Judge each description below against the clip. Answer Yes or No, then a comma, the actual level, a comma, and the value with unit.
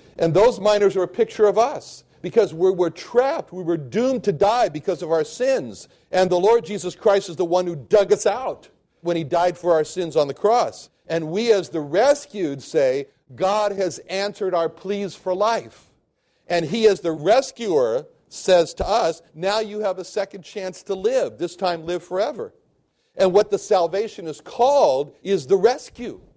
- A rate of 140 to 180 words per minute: No, average, 190 wpm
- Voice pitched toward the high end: Yes, high, 195 Hz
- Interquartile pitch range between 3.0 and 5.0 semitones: Yes, average, 3.8 semitones